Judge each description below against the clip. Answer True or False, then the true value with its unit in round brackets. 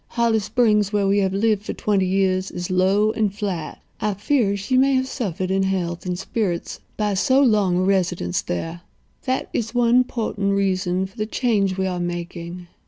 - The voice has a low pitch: False (195 Hz)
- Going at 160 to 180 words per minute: False (190 wpm)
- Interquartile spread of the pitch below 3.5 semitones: True (2.9 semitones)